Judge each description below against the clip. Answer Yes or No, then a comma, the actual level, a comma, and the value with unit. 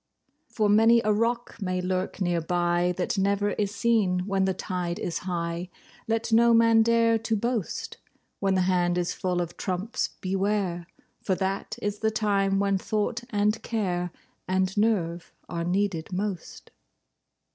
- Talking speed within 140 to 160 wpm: Yes, average, 150 wpm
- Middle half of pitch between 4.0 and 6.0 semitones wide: No, average, 3.2 semitones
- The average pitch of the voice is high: Yes, high, 195 Hz